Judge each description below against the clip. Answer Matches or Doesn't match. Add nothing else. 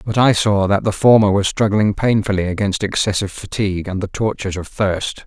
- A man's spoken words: Matches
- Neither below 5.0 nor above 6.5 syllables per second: Matches